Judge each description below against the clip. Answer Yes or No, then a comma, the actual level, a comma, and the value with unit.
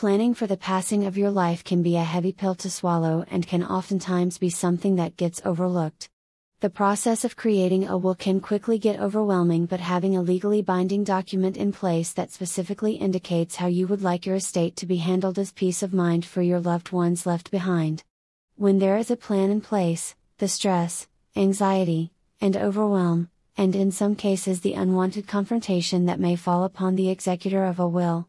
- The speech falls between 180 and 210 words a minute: Yes, average, 190 wpm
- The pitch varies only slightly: Yes, narrow, 2.0 semitones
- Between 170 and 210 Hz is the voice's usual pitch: Yes, medium, 185 Hz